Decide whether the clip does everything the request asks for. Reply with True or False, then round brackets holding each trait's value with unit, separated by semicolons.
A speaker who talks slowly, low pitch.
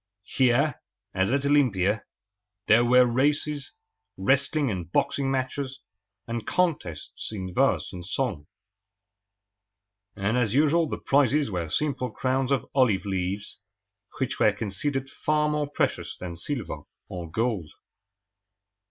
True (120 wpm; 125 Hz)